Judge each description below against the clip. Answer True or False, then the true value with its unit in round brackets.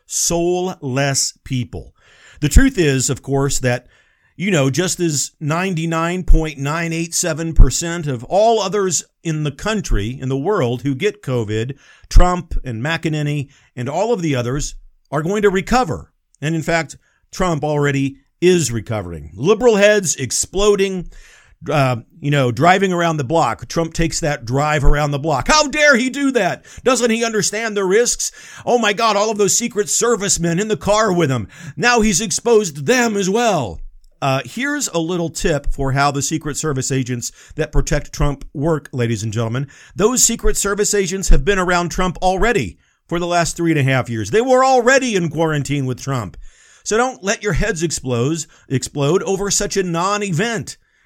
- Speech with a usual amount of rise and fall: False (6.5 semitones)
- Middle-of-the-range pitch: True (165 Hz)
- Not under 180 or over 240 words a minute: False (170 wpm)